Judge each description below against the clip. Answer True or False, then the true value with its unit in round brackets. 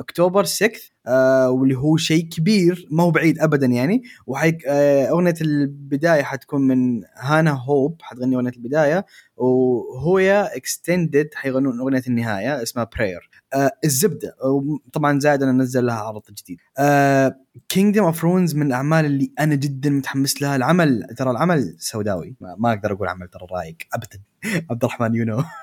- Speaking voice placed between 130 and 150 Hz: True (140 Hz)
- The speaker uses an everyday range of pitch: True (4.0 semitones)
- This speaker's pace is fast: True (150 wpm)